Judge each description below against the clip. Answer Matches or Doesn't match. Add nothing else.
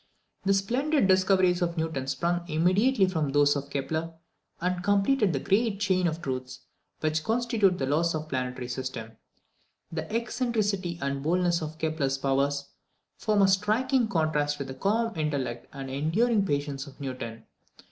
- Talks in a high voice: Doesn't match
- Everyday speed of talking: Matches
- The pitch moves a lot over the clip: Matches